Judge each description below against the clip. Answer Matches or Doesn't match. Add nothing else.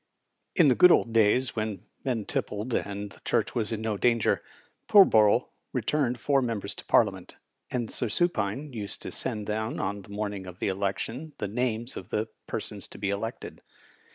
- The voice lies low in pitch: Matches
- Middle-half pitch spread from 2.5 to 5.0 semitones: Matches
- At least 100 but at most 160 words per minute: Doesn't match